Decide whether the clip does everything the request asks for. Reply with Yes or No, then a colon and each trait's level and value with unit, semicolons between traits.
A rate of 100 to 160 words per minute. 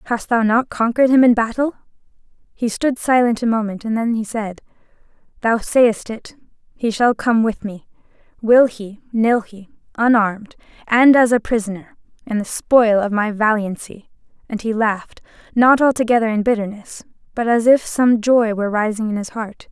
No: average, 170 wpm